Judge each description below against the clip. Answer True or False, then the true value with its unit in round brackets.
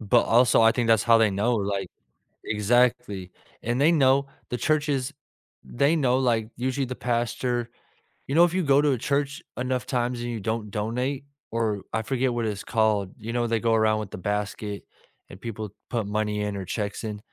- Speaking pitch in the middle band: False (115 Hz)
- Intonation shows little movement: False (3.2 semitones)